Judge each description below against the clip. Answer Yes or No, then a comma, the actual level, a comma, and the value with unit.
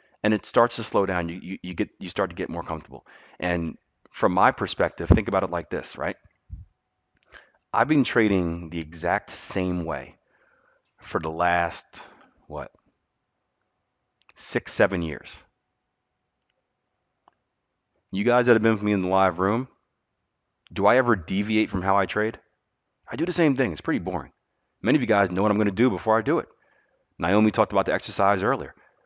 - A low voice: Yes, low, 100 Hz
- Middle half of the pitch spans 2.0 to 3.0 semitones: No, average, 3.7 semitones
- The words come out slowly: No, average, 180 wpm